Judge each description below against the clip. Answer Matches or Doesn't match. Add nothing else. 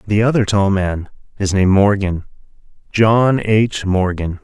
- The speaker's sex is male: Matches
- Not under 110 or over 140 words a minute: Matches